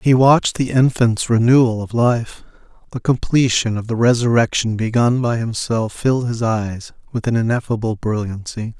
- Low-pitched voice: Yes, low, 115 Hz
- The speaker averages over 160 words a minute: No, average, 150 wpm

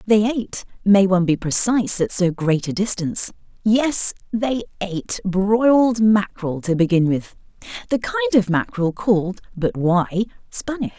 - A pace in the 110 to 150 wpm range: Yes, average, 140 wpm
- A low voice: No, high, 205 Hz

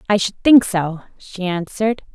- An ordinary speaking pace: Yes, average, 170 wpm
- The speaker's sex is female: Yes, female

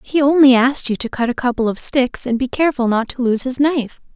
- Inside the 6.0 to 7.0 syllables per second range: Yes, 6.1 syllables/s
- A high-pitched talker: Yes, very high, 255 Hz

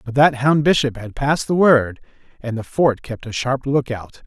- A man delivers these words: Yes, male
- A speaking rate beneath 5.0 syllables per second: Yes, 4.8 syllables/s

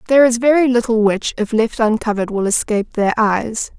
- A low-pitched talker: No, high, 225 Hz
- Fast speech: No, average, 190 wpm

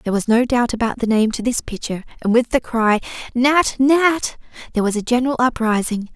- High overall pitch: Yes, high, 235 Hz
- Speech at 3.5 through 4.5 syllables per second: No, 5.8 syllables/s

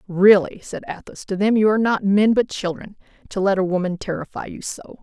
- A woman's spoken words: Yes, female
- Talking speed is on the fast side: Yes, fast, 215 wpm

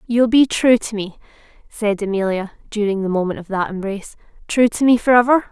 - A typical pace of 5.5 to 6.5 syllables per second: Yes, 5.7 syllables/s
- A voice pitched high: Yes, high, 215 Hz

